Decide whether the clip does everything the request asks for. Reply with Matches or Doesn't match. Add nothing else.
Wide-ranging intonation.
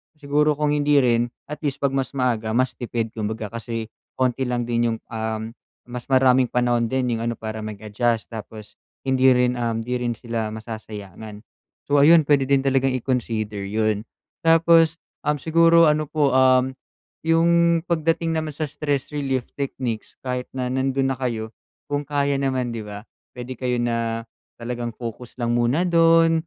Doesn't match